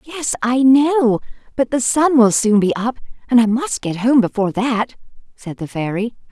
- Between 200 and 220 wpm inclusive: No, average, 190 wpm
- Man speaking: No, female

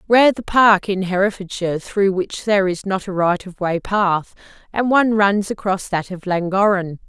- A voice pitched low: No, high, 195 Hz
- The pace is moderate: Yes, average, 185 wpm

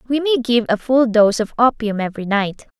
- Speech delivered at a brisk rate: Yes, fast, 215 wpm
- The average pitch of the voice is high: Yes, high, 230 Hz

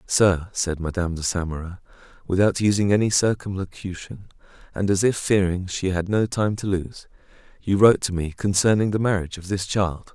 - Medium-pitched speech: No, very low, 95 Hz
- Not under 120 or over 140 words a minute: No, average, 175 wpm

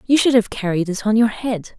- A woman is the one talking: Yes, female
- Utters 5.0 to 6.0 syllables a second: Yes, 5.4 syllables/s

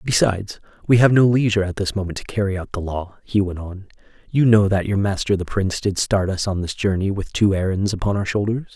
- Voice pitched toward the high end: No, low, 100 Hz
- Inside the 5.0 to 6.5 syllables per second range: Yes, 6.0 syllables/s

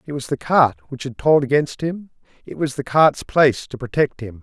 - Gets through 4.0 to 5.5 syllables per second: Yes, 5.2 syllables/s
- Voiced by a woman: No, male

